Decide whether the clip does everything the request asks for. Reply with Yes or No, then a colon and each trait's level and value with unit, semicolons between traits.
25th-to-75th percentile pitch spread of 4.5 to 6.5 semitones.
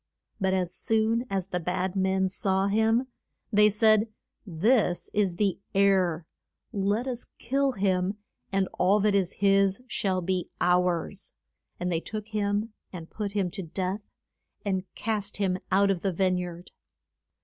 No: narrow, 2.4 semitones